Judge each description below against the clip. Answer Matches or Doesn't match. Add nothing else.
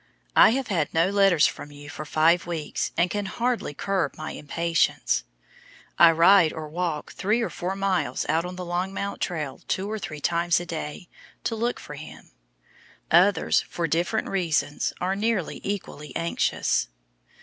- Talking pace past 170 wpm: Doesn't match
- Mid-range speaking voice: Matches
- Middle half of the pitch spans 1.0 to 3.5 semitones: Doesn't match